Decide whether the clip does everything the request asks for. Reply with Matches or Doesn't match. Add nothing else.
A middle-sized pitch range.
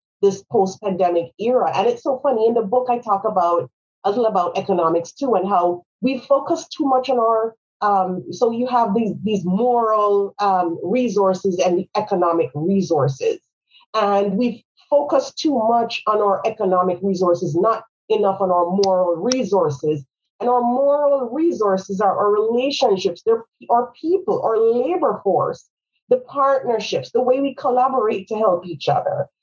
Matches